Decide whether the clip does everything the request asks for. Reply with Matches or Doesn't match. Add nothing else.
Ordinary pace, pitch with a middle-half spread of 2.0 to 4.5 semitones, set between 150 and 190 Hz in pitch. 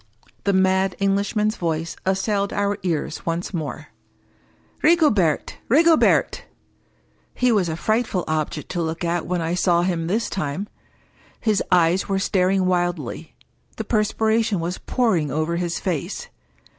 Doesn't match